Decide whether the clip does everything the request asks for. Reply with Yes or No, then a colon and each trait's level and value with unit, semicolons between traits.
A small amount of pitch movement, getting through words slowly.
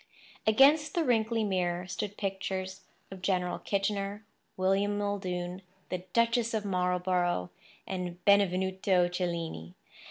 Yes: narrow, 2.3 semitones; slow, 105 wpm